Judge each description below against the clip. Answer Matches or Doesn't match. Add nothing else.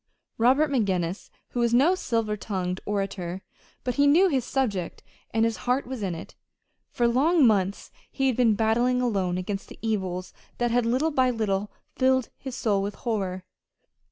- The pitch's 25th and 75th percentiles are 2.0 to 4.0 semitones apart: Doesn't match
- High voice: Matches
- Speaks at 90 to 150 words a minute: Doesn't match